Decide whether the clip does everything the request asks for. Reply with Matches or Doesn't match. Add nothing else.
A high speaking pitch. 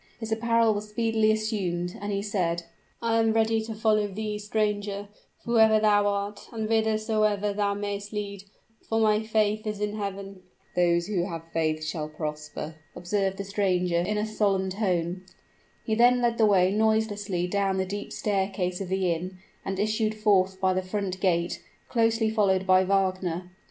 Matches